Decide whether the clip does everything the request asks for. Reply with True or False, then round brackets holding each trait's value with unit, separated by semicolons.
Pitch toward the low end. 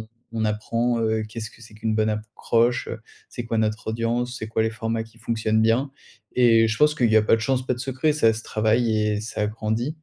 True (115 Hz)